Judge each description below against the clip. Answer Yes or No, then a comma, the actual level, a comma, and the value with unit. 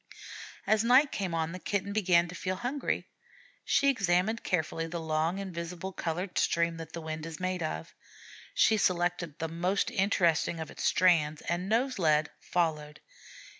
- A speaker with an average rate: Yes, average, 160 wpm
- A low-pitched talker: No, medium, 175 Hz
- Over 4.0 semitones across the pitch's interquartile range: No, average, 3.0 semitones